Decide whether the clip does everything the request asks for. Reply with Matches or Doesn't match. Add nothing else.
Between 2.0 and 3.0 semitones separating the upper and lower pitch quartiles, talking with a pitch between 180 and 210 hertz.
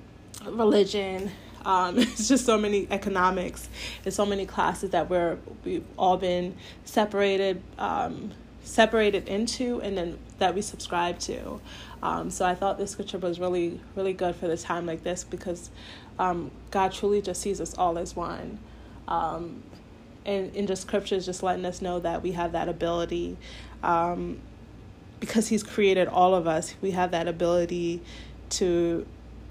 Matches